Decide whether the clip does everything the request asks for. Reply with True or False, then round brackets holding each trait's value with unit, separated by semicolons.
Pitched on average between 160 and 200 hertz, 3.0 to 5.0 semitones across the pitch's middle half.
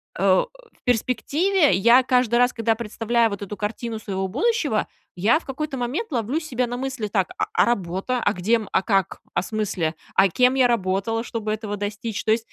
False (225 Hz; 3.7 semitones)